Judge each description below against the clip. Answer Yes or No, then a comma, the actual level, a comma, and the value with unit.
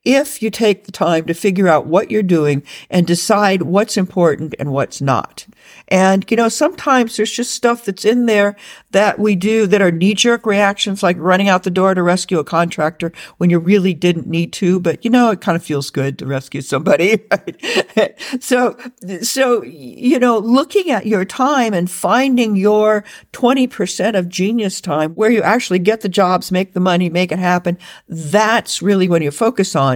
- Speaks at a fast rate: No, average, 190 wpm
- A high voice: Yes, high, 195 Hz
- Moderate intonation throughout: Yes, average, 4.2 semitones